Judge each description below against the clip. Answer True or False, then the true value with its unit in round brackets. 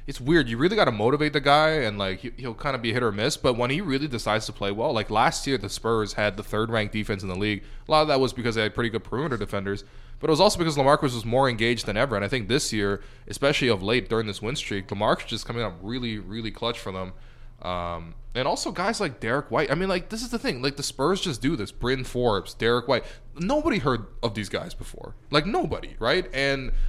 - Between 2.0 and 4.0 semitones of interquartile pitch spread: False (5.0 semitones)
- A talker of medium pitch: False (120 Hz)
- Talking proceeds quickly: True (260 wpm)